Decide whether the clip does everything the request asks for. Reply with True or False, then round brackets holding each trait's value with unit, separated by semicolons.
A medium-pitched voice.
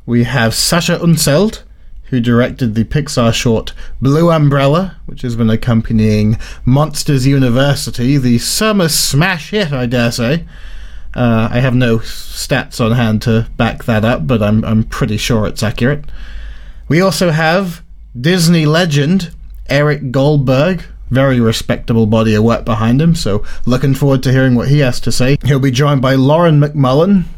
False (130 Hz)